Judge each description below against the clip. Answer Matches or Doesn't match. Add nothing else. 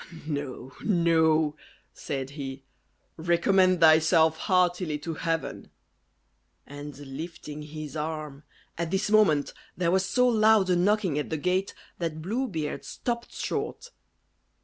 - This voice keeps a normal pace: Doesn't match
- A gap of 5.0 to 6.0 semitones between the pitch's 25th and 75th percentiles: Doesn't match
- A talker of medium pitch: Matches